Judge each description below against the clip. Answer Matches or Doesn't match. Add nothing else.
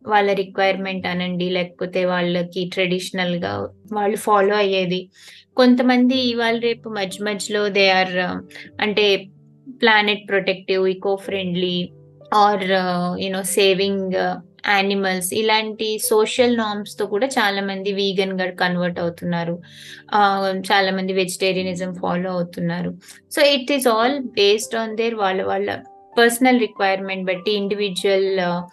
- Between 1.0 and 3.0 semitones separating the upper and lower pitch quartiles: Matches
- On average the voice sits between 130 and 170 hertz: Doesn't match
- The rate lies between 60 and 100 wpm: Doesn't match